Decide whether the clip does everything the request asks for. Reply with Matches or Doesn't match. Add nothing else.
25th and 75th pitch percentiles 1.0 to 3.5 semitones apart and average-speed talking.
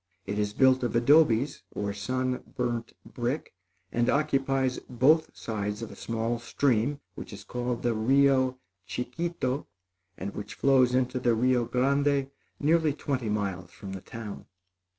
Matches